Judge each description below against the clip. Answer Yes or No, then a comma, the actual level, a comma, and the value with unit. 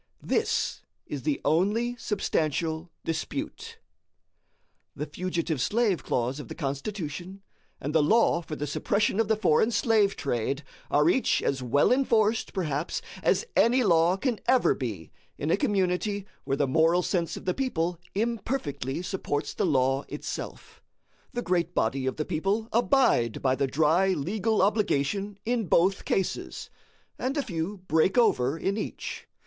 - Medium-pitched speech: Yes, medium, 180 Hz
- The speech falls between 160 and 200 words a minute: No, average, 150 wpm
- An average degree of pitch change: No, wide, 6.5 semitones